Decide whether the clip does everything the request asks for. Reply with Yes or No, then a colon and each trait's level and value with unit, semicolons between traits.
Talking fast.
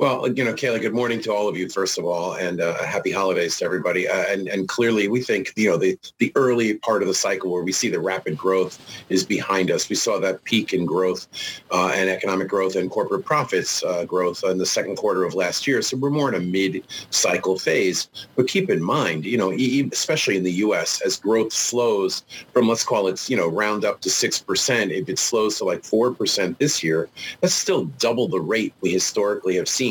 Yes: fast, 230 wpm